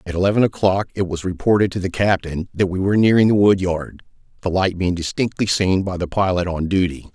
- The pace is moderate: No, fast, 210 wpm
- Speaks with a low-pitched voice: Yes, very low, 95 Hz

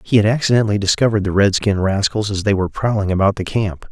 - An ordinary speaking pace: No, fast, 230 wpm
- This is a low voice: Yes, low, 100 Hz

